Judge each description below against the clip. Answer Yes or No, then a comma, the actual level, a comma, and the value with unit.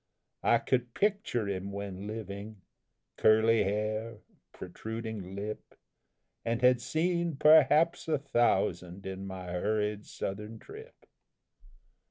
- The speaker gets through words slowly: Yes, slow, 105 wpm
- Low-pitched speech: Yes, low, 110 Hz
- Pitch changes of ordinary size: Yes, average, 4.0 semitones